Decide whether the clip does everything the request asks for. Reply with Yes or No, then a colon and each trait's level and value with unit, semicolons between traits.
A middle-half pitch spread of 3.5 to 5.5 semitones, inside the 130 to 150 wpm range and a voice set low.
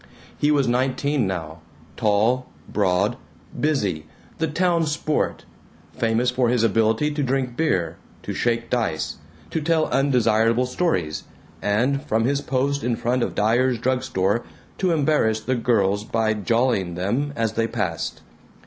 Yes: average, 4.3 semitones; average, 140 wpm; low, 120 Hz